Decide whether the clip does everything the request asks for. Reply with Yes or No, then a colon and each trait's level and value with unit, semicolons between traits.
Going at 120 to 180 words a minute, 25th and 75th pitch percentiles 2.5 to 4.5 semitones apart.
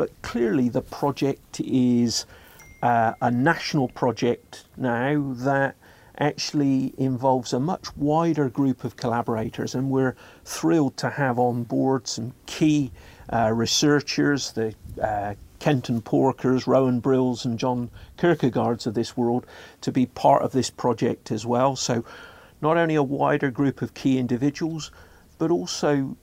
Yes: average, 140 wpm; average, 3.0 semitones